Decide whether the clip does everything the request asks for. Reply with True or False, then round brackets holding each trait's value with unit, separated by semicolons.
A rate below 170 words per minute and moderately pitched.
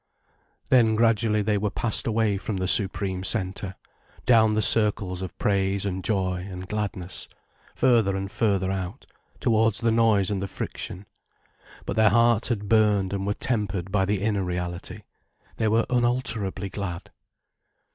False (150 wpm; 100 Hz)